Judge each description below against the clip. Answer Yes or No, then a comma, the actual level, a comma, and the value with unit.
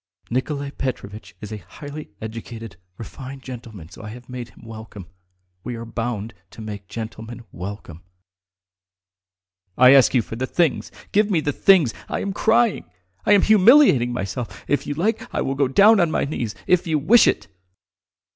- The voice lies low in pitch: Yes, low, 125 Hz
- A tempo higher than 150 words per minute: Yes, average, 165 wpm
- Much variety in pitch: Yes, wide, 5.8 semitones